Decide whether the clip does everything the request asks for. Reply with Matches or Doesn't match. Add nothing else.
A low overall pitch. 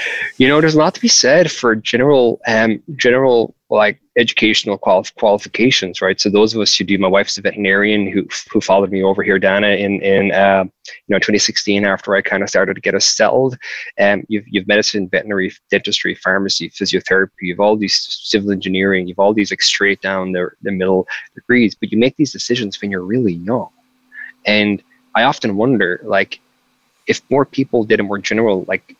Matches